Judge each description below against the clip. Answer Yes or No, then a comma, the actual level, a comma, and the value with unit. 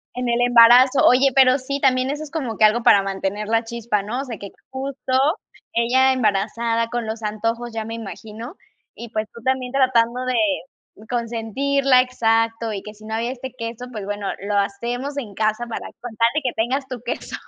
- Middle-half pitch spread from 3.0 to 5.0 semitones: No, narrow, 2.6 semitones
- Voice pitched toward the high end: Yes, high, 235 Hz